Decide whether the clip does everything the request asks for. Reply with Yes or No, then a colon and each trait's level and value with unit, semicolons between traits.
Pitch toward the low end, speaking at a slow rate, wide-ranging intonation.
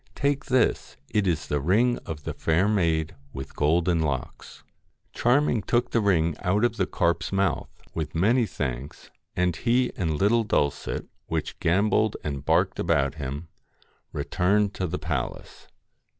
No: very low, 90 Hz; average, 150 wpm; wide, 5.7 semitones